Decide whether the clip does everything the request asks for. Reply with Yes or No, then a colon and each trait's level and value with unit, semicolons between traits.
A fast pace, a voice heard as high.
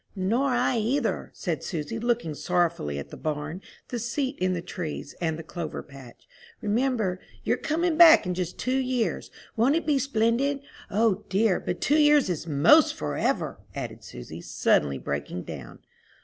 No: average, 165 wpm; high, 205 Hz